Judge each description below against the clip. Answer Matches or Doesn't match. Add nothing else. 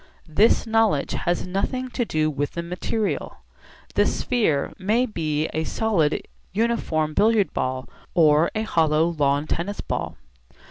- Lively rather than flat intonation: Matches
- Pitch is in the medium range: Matches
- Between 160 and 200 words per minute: Doesn't match